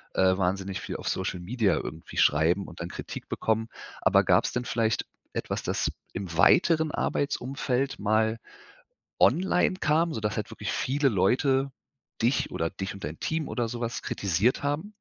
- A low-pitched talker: Yes, low, 115 Hz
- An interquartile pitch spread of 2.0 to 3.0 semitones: No, wide, 6.5 semitones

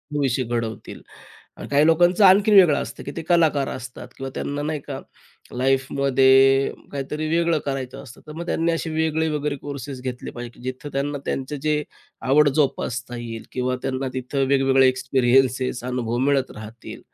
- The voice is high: No, low, 135 Hz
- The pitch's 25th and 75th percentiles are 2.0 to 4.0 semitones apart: Yes, average, 2.8 semitones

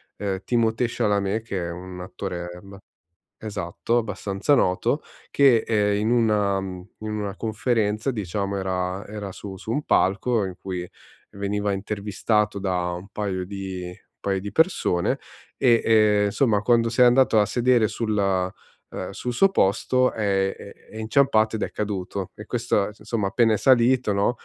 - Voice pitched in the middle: No, low, 105 Hz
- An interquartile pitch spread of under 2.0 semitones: No, average, 2.8 semitones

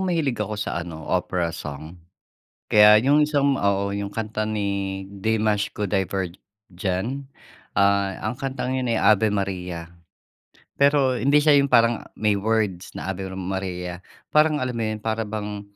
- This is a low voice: Yes, low, 105 Hz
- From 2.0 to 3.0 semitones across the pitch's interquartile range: No, average, 3.7 semitones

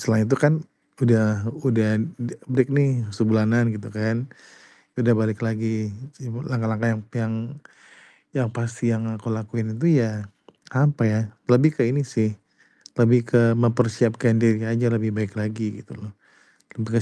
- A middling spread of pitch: No, narrow, 1.8 semitones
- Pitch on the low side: Yes, low, 115 Hz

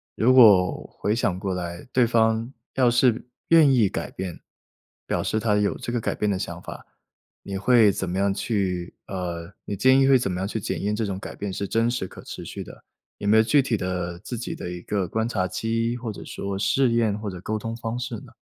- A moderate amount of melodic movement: Yes, average, 3.7 semitones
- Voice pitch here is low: Yes, low, 105 Hz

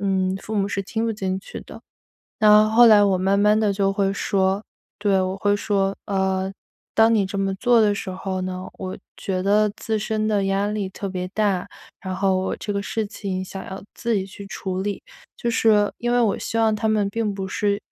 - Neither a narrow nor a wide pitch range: No, narrow, 1.8 semitones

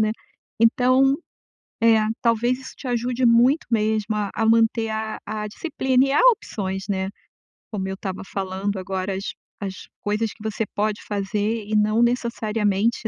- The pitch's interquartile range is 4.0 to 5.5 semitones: No, narrow, 2.5 semitones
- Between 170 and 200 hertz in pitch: No, high, 220 Hz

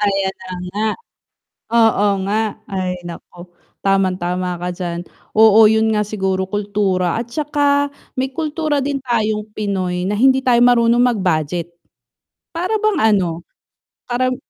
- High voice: Yes, high, 210 Hz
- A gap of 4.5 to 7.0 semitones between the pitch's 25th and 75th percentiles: Yes, average, 4.8 semitones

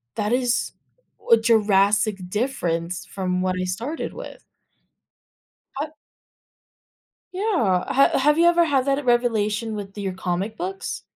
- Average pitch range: No, wide, 5.9 semitones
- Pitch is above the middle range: Yes, high, 215 Hz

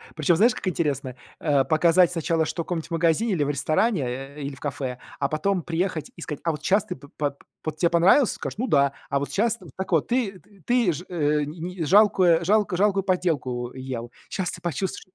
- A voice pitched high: No, medium, 165 Hz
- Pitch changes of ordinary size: Yes, average, 4.5 semitones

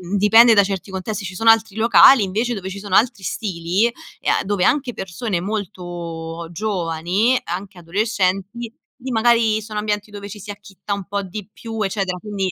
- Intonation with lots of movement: No, average, 2.9 semitones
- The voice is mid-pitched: No, high, 205 Hz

